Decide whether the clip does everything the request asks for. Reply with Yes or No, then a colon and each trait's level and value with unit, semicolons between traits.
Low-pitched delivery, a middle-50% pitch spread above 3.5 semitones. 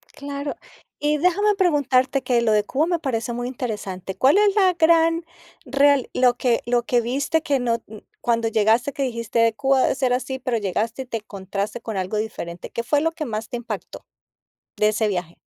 No: high, 245 Hz; average, 4.2 semitones